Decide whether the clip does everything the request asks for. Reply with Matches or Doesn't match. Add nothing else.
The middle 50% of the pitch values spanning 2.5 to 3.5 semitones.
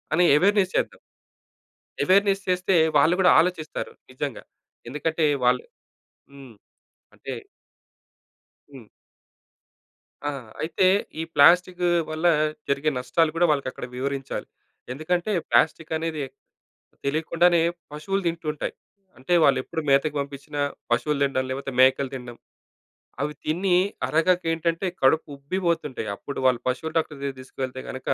Doesn't match